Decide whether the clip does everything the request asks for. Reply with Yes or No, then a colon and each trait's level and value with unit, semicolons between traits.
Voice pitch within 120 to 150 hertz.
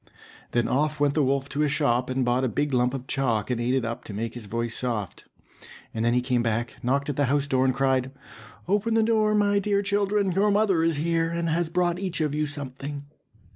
Yes: medium, 140 Hz